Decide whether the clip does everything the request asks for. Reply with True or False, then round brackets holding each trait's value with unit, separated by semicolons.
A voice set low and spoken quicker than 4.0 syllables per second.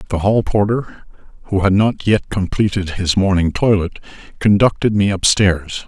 True (100 Hz; 4.6 syllables/s)